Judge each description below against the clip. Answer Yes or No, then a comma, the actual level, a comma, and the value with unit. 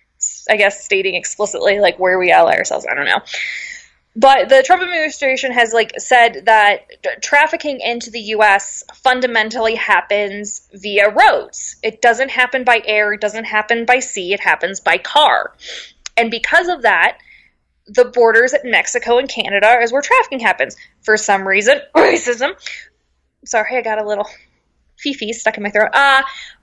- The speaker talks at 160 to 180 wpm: Yes, average, 165 wpm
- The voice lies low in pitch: No, high, 235 Hz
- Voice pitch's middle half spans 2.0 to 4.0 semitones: No, average, 4.6 semitones